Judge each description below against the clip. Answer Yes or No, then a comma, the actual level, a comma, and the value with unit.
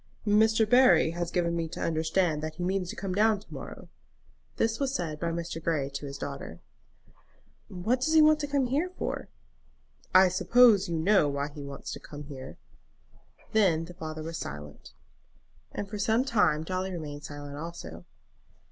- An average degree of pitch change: No, wide, 5.8 semitones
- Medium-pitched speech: Yes, medium, 170 Hz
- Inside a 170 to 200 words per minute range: Yes, average, 175 wpm